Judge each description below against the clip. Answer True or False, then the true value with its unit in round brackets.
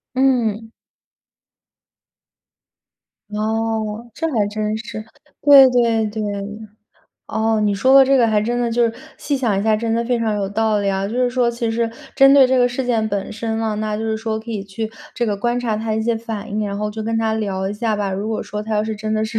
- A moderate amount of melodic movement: False (1.9 semitones)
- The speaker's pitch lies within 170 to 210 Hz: False (220 Hz)